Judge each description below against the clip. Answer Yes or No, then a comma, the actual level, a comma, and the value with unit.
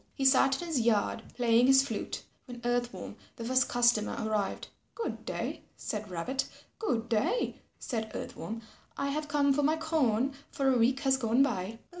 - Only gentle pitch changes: No, average, 3.4 semitones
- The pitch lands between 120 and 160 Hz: No, very high, 250 Hz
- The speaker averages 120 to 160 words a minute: No, average, 180 wpm